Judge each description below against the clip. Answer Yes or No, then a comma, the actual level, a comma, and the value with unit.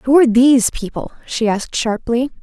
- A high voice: Yes, high, 240 Hz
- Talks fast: No, average, 175 wpm